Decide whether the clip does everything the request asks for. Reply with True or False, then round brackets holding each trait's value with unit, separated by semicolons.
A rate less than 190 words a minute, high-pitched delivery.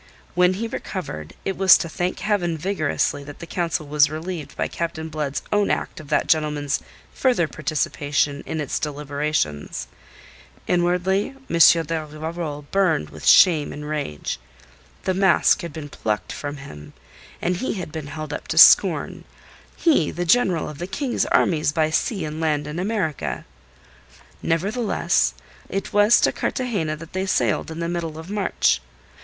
False (160 wpm; 160 Hz)